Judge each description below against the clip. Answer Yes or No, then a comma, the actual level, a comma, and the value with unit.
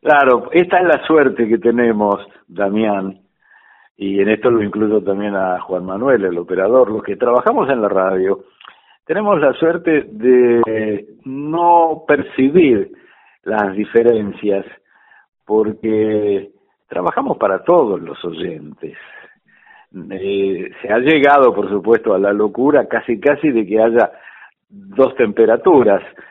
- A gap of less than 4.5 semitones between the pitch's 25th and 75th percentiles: No, average, 4.8 semitones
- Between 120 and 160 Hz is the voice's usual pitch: No, low, 110 Hz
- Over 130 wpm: No, slow, 125 wpm